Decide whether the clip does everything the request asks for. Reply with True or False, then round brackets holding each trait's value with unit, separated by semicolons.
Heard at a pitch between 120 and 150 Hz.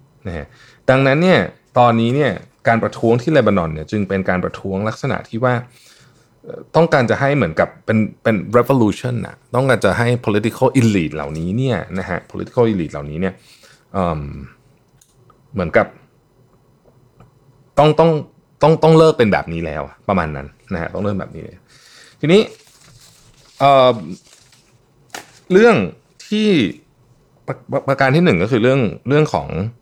True (125 Hz)